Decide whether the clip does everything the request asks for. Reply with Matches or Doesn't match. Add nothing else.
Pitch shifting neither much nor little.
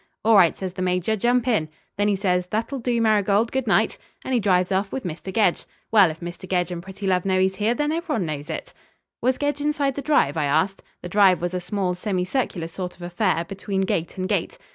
Matches